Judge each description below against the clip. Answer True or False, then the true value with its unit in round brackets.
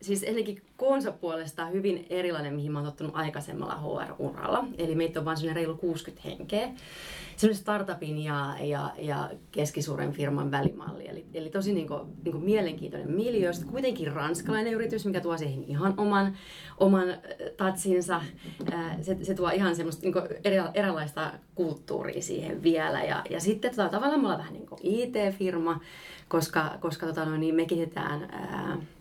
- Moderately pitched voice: True (175 Hz)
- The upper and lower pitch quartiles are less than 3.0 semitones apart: False (3.3 semitones)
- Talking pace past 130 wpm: True (150 wpm)